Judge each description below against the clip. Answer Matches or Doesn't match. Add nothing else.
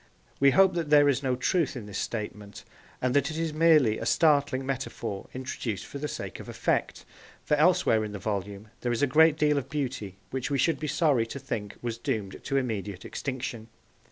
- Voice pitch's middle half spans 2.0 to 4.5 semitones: Doesn't match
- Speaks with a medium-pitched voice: Doesn't match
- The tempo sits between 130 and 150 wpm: Doesn't match